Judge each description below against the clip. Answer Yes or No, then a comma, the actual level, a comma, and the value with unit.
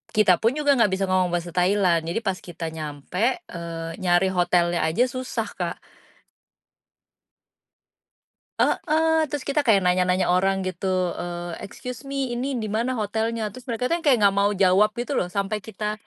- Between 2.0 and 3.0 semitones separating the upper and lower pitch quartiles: No, wide, 5.4 semitones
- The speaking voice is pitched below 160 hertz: No, high, 195 Hz